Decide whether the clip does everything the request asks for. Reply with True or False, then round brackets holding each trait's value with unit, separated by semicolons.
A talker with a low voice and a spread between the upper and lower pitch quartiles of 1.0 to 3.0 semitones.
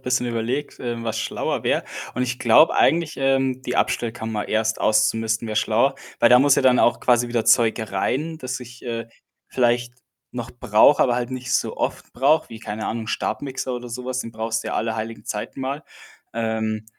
True (120 Hz; 2.4 semitones)